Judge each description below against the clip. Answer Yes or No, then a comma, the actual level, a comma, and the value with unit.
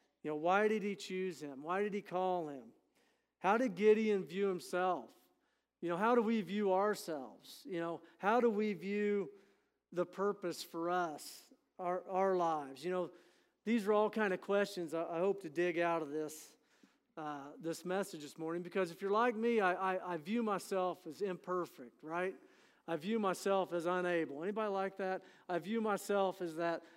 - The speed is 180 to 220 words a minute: Yes, average, 185 wpm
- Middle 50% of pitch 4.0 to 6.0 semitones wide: No, average, 3.1 semitones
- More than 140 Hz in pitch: Yes, medium, 185 Hz